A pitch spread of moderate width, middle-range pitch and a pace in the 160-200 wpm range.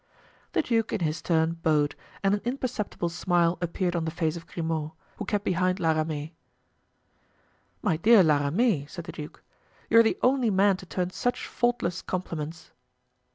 Yes: average, 4.3 semitones; medium, 175 Hz; average, 170 wpm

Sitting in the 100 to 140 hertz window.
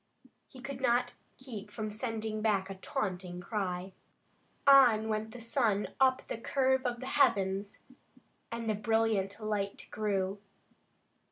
No: high, 215 Hz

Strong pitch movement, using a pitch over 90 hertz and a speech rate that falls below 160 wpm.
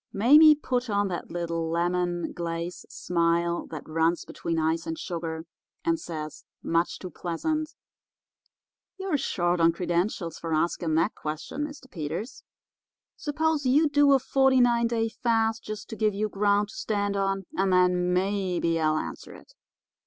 Yes: wide, 5.8 semitones; medium, 185 Hz; average, 150 wpm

